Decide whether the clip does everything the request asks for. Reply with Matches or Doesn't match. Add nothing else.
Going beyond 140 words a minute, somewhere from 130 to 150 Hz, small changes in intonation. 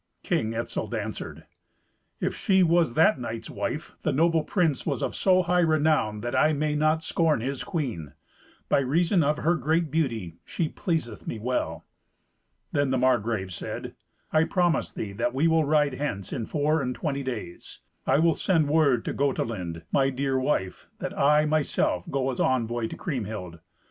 Doesn't match